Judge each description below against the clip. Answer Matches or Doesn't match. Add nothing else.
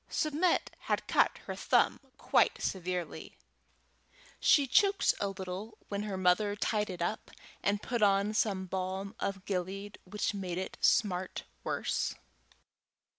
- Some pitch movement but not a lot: Doesn't match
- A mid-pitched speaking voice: Doesn't match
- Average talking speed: Doesn't match